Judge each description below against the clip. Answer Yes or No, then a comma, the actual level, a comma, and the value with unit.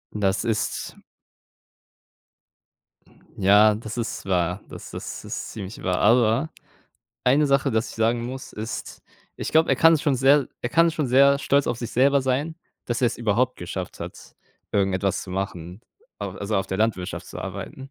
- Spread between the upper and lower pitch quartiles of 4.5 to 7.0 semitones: Yes, average, 5.2 semitones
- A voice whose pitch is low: Yes, low, 115 Hz